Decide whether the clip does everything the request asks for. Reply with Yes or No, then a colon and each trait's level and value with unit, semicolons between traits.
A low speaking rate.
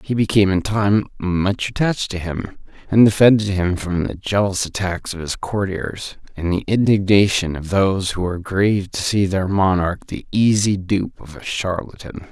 No: average, 175 wpm